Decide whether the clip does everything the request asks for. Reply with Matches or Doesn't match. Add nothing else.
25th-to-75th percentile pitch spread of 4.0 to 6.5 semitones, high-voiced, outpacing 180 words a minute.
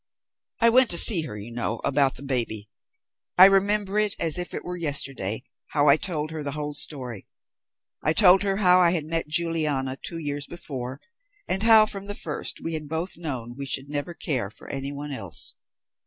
Doesn't match